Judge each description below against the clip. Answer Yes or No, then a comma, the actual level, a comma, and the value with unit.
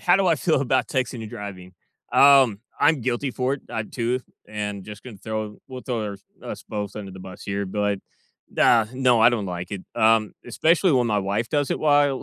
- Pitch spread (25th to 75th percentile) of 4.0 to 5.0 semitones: Yes, average, 4.3 semitones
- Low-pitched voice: Yes, low, 115 Hz